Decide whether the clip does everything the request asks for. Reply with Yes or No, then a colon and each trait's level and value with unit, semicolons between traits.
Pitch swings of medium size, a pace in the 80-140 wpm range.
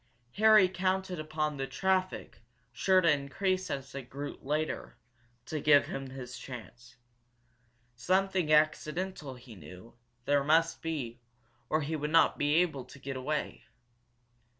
Yes: average, 5.0 semitones; slow, 135 wpm